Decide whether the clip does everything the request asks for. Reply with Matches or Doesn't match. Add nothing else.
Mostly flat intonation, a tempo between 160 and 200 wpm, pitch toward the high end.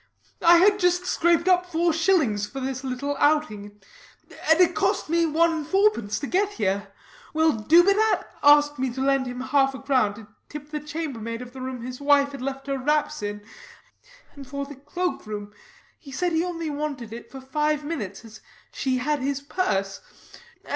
Doesn't match